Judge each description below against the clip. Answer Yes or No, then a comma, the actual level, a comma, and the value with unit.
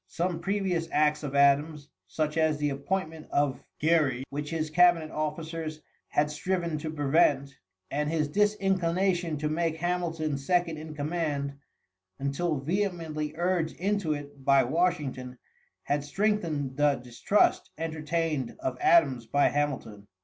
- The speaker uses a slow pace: Yes, slow, 130 wpm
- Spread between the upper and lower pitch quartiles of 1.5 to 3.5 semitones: Yes, average, 2.9 semitones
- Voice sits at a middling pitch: Yes, medium, 155 Hz